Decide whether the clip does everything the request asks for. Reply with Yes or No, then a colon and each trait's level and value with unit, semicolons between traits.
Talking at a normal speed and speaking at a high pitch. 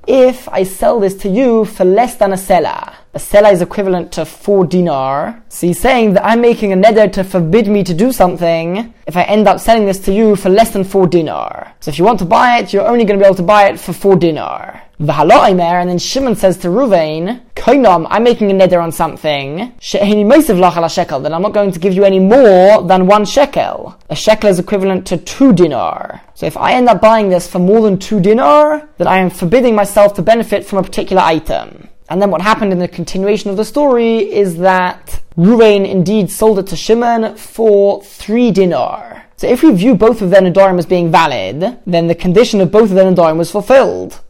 No: fast, 220 wpm; high, 200 Hz